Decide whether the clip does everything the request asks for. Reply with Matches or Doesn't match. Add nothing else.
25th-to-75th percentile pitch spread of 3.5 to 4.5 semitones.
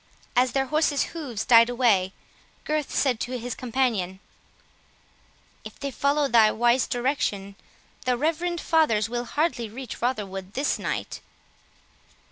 Matches